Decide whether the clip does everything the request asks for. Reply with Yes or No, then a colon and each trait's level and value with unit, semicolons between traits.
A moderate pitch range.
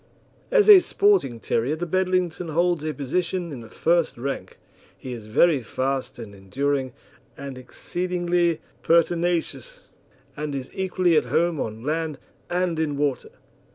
Yes: average, 4.8 semitones